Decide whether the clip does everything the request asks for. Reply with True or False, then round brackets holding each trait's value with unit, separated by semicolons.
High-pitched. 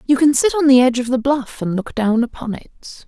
True (255 Hz)